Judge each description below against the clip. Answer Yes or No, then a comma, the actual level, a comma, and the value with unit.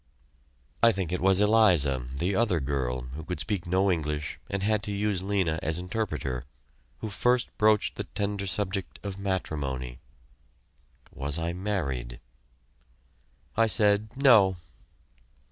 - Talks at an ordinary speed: No, slow, 130 wpm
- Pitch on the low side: Yes, very low, 95 Hz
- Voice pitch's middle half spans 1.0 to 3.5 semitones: No, wide, 5.5 semitones